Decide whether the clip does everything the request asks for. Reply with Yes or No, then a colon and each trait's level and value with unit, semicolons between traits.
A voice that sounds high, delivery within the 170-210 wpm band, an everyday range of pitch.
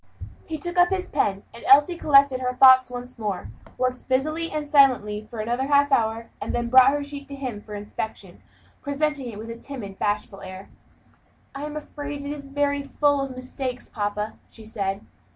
Yes: very high, 260 Hz; average, 190 wpm; average, 4.5 semitones